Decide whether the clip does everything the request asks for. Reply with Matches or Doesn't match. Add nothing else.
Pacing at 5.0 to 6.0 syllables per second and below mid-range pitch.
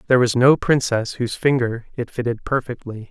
Matches